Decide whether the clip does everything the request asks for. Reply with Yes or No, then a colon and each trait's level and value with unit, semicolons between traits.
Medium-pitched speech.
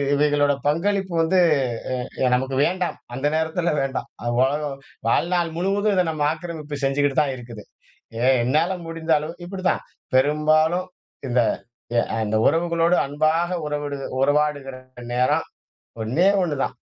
Yes: medium, 150 Hz